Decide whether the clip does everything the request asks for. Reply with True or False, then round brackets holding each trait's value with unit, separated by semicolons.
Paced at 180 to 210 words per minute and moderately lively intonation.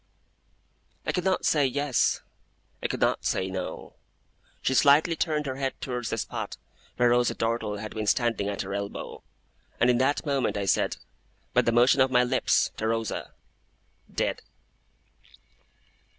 False (155 wpm; 4.0 semitones)